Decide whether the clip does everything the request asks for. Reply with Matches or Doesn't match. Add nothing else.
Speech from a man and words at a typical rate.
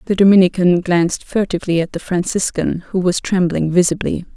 Doesn't match